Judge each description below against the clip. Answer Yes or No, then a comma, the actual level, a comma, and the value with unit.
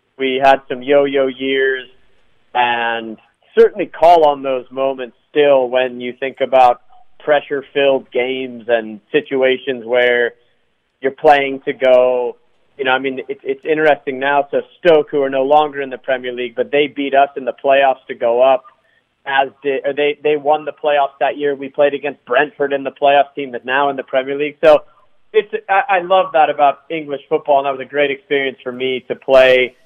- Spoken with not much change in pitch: Yes, narrow, 2.0 semitones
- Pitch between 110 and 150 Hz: Yes, low, 135 Hz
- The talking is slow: No, average, 195 wpm